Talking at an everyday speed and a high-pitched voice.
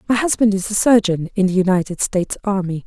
No: fast, 210 wpm; high, 200 Hz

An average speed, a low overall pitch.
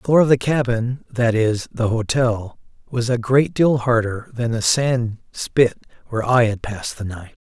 Yes: average, 180 wpm; low, 120 Hz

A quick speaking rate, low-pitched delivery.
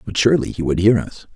Yes: fast, 265 wpm; low, 100 Hz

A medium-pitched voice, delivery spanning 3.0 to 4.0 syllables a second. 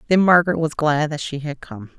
No: medium, 160 Hz; 5.8 syllables/s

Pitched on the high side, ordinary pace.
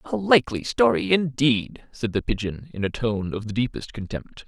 No: low, 120 Hz; average, 190 wpm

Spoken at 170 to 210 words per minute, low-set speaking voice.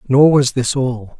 Yes: average, 200 wpm; low, 130 Hz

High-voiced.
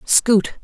Yes: high, 220 Hz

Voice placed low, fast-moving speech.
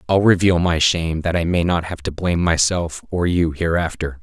Yes: very low, 85 Hz; fast, 215 wpm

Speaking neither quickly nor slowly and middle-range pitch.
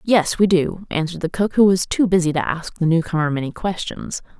No: fast, 230 wpm; medium, 175 Hz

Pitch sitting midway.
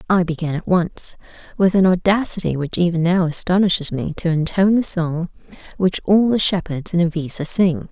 Yes: medium, 175 Hz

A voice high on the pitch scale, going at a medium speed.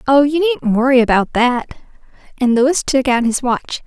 Yes: very high, 260 Hz; average, 185 wpm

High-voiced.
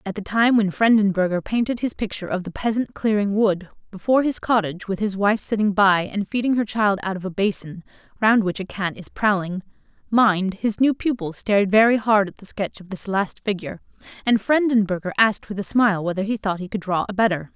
Yes: high, 205 Hz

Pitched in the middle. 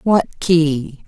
Yes: medium, 160 Hz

